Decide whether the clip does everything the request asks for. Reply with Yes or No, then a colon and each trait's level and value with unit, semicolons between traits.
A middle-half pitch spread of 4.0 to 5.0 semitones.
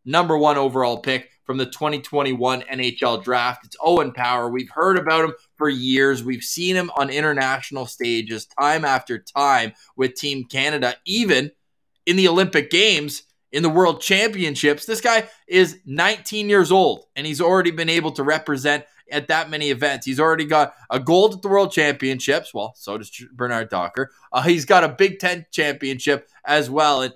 Yes: average, 4.5 semitones